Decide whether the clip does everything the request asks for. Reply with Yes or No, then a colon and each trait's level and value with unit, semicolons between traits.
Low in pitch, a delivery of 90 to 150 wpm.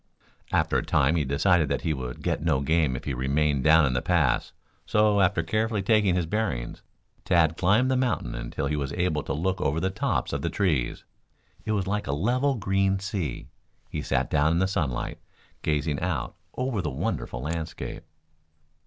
No: very low, 80 Hz; average, 190 wpm